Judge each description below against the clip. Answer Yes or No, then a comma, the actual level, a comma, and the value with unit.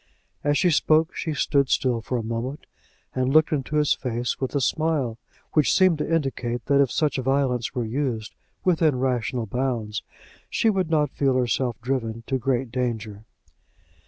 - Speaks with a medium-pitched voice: No, low, 130 Hz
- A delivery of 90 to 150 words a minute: No, average, 165 wpm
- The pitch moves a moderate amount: Yes, average, 3.7 semitones